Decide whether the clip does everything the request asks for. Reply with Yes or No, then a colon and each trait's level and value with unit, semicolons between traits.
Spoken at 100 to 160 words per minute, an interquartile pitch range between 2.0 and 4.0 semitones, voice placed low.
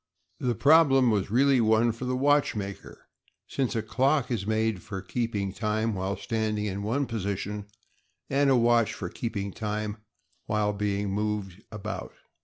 Yes: average, 150 wpm; average, 3.1 semitones; low, 110 Hz